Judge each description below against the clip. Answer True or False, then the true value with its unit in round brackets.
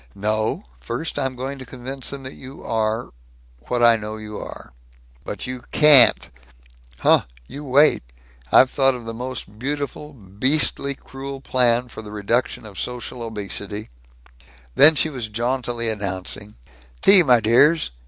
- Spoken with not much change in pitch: False (3.8 semitones)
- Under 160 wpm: True (150 wpm)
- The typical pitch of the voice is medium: False (125 Hz)